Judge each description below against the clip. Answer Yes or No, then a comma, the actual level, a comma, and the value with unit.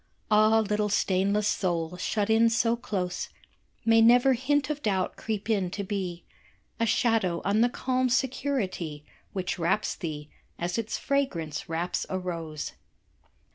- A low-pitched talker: No, high, 205 Hz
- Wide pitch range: No, average, 4.4 semitones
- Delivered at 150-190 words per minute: No, average, 140 wpm